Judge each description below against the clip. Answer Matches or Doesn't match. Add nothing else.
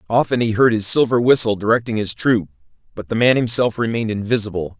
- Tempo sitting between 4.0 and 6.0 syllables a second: Doesn't match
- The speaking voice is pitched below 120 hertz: Matches